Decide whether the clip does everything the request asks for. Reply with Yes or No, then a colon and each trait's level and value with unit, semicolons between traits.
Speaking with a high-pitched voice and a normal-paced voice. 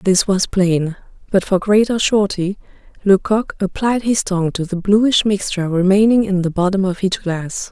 Yes: high, 195 Hz; average, 170 wpm